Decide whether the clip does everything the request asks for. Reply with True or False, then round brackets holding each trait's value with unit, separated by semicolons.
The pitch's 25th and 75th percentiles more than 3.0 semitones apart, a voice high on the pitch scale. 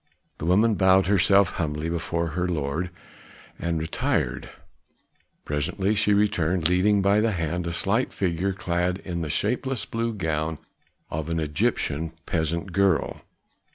False (3.4 semitones; 90 Hz)